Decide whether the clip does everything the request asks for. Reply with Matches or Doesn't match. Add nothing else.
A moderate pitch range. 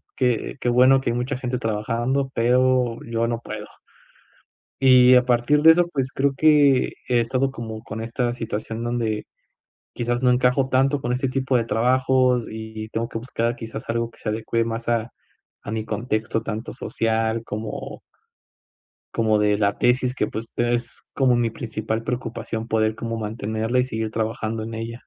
Doesn't match